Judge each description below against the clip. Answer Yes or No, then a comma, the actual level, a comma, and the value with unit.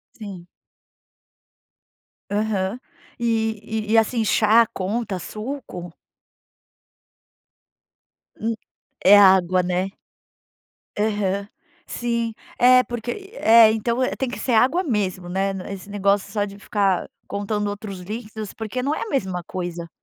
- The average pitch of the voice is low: No, high, 210 Hz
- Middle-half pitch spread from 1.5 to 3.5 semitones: Yes, average, 3.2 semitones